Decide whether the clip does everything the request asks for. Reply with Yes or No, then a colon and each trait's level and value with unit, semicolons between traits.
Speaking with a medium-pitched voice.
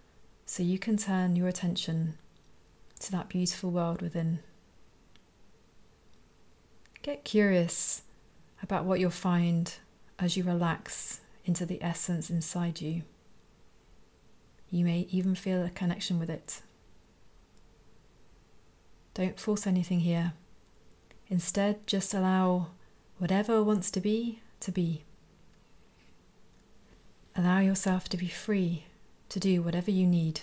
Yes: medium, 180 Hz